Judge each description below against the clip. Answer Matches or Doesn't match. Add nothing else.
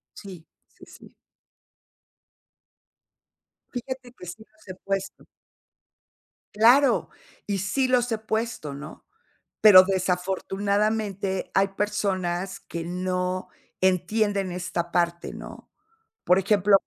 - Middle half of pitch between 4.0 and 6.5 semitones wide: Doesn't match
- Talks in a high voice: Matches